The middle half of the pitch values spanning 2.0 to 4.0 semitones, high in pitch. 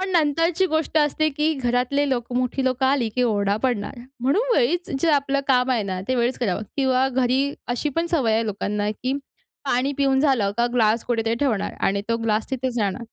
Yes: average, 3.6 semitones; very high, 255 Hz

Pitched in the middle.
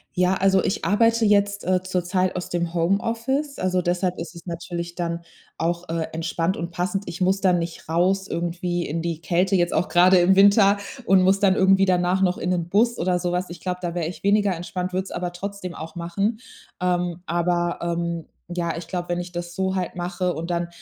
Yes: medium, 180 Hz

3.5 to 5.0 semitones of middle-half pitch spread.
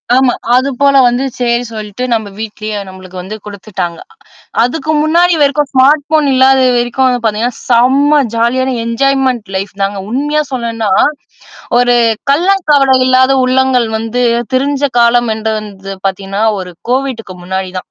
Yes: average, 3.9 semitones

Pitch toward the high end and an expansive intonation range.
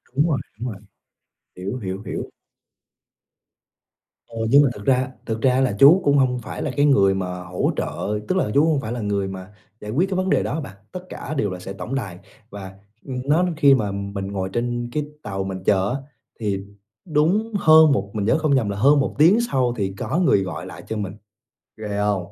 No: low, 115 Hz; wide, 6.3 semitones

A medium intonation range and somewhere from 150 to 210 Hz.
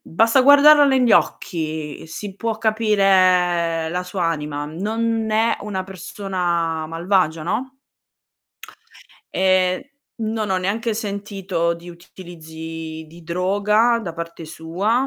Yes: average, 4.5 semitones; medium, 185 Hz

